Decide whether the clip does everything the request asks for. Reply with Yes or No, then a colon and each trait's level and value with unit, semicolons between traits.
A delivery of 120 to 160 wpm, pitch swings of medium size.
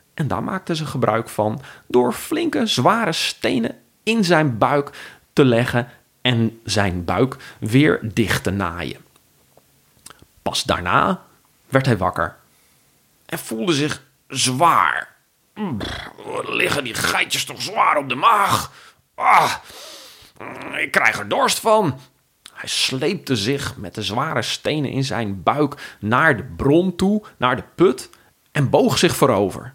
No: slow, 135 wpm; wide, 5.7 semitones